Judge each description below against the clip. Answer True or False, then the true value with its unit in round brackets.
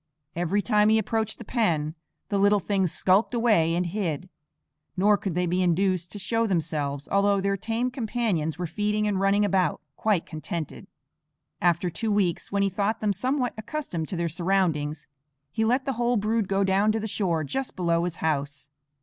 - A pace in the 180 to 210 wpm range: True (185 wpm)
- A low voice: False (195 Hz)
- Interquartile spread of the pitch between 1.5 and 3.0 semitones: False (4.0 semitones)